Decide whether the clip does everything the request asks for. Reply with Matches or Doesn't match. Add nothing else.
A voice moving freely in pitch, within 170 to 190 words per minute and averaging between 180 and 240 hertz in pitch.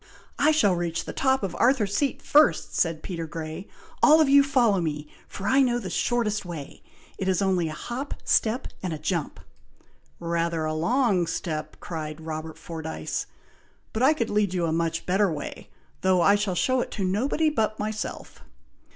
Matches